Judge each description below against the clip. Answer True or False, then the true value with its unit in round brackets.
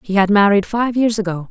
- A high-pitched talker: True (205 Hz)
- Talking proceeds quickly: True (240 wpm)